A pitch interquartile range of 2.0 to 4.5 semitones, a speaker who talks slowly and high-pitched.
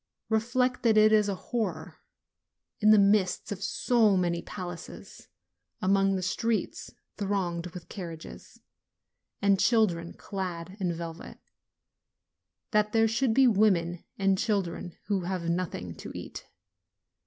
Yes: average, 3.5 semitones; slow, 125 wpm; high, 195 Hz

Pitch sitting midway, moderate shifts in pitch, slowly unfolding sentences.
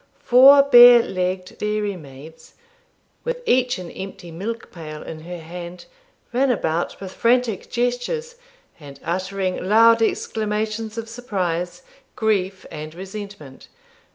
No: high, 200 Hz; average, 5.0 semitones; slow, 120 wpm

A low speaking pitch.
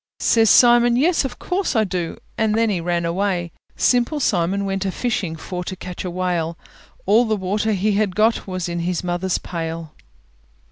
No: high, 190 Hz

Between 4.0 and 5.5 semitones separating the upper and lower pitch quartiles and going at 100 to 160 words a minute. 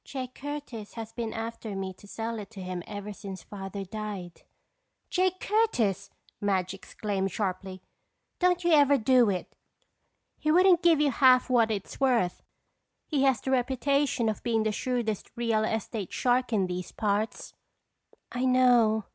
Yes: average, 4.4 semitones; average, 155 wpm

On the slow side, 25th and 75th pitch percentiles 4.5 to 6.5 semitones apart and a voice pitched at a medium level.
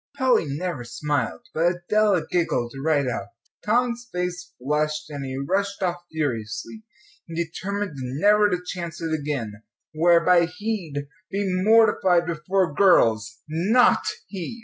Yes: slow, 125 wpm; average, 5.0 semitones; medium, 170 Hz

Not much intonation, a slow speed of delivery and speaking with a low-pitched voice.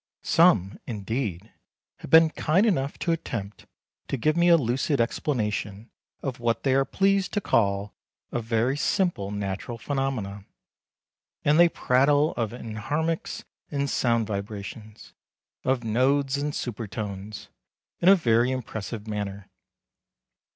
No: wide, 5.6 semitones; slow, 130 wpm; low, 120 Hz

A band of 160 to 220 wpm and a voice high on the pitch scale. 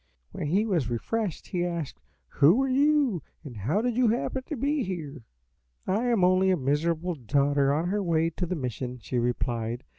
No: average, 185 wpm; medium, 170 Hz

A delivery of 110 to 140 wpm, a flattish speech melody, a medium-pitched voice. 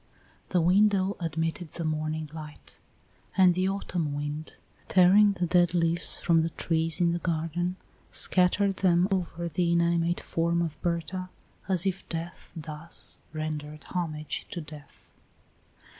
Yes: slow, 135 wpm; narrow, 2.3 semitones; medium, 170 Hz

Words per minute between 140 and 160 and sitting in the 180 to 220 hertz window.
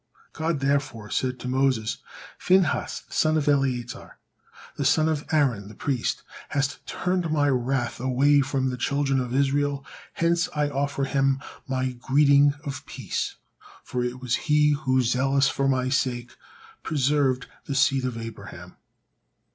No: average, 145 wpm; low, 135 Hz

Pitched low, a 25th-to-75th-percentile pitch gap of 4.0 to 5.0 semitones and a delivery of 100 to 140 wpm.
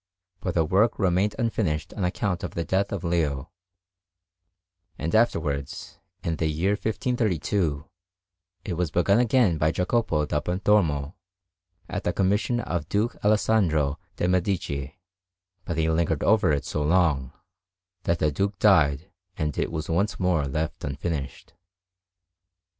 Yes: very low, 85 Hz; average, 4.7 semitones; slow, 135 wpm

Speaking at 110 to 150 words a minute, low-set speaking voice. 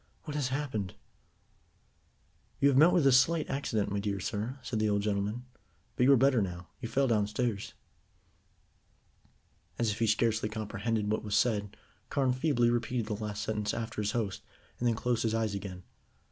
No: average, 175 wpm; low, 110 Hz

